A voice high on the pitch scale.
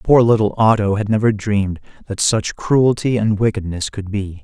No: low, 105 Hz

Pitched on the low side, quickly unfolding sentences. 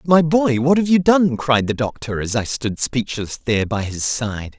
Yes: low, 130 Hz; fast, 220 wpm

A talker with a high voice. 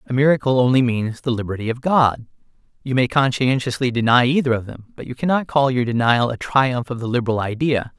No: low, 125 Hz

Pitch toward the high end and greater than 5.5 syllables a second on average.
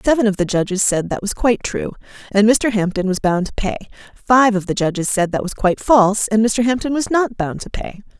Yes: high, 210 Hz; 5.8 syllables/s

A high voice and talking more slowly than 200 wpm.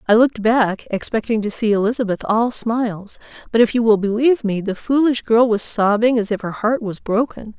No: high, 225 Hz; fast, 205 wpm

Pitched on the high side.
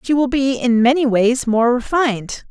Yes: very high, 250 Hz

